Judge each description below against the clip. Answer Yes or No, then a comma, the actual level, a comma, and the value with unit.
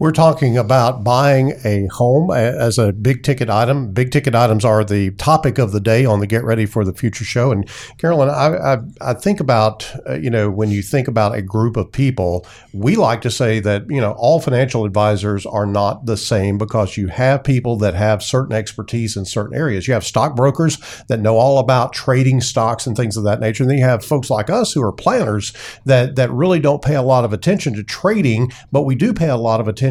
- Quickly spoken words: Yes, fast, 230 wpm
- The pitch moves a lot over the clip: No, average, 3.8 semitones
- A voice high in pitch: No, low, 120 Hz